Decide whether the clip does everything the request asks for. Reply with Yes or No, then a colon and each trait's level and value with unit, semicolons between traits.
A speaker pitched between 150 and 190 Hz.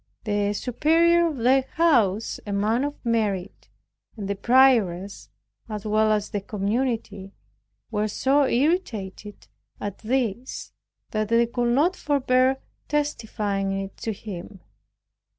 No: high, 220 Hz